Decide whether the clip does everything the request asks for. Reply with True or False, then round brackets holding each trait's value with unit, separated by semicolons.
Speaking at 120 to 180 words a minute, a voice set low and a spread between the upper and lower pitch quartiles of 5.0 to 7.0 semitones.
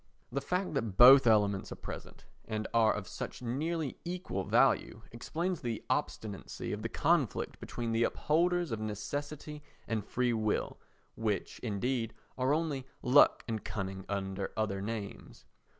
True (145 wpm; 115 Hz; 5.3 semitones)